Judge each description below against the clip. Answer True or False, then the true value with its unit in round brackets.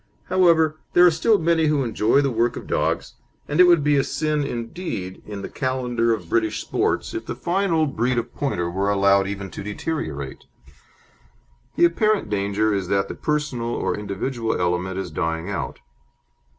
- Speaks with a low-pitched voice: True (120 Hz)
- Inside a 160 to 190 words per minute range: True (175 wpm)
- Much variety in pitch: True (7.5 semitones)